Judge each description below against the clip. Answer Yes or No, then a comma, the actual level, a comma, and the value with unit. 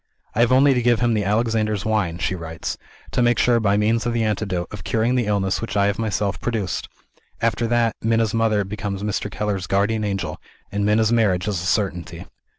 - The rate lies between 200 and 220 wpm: Yes, fast, 205 wpm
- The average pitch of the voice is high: No, low, 105 Hz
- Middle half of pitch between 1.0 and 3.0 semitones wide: Yes, narrow, 2.6 semitones